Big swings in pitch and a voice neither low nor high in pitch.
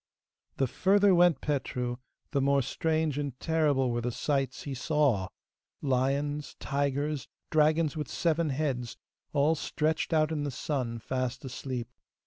No: average, 3.1 semitones; medium, 145 Hz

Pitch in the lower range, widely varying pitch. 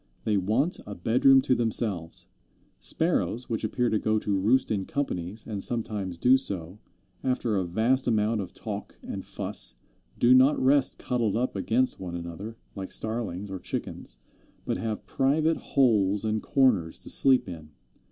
No: low, 110 Hz; average, 4.7 semitones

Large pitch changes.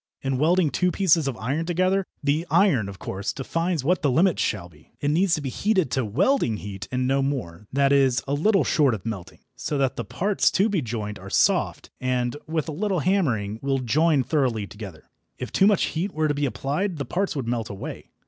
Yes: wide, 6.3 semitones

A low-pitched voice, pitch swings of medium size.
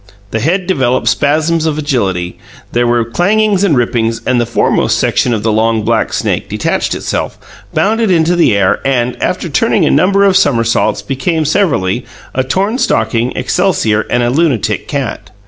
No: low, 130 Hz; wide, 7.0 semitones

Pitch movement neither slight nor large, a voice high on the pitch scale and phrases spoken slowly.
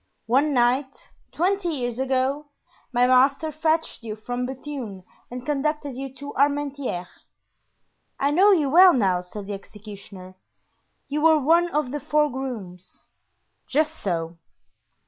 Yes: average, 4.7 semitones; very high, 270 Hz; slow, 130 wpm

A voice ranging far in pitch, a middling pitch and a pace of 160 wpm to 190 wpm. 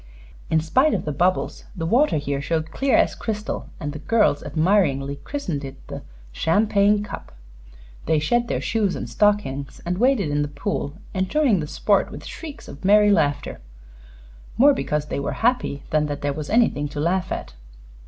Yes: wide, 6.4 semitones; medium, 170 Hz; average, 175 wpm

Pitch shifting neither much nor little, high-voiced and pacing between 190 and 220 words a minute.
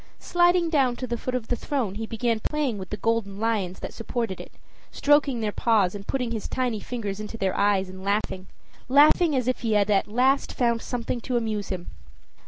Yes: average, 3.8 semitones; high, 230 Hz; fast, 205 wpm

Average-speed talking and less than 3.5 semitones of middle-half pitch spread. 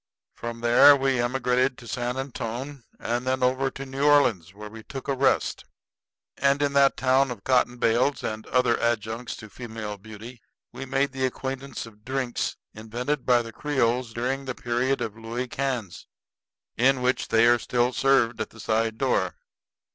Yes: average, 170 wpm; average, 2.8 semitones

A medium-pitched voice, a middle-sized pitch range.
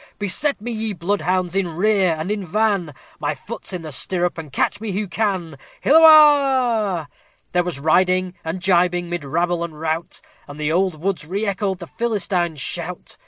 Yes: medium, 180 Hz; average, 3.7 semitones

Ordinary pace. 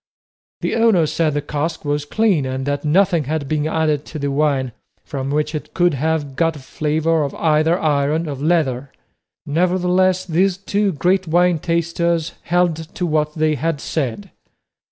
Yes: average, 165 wpm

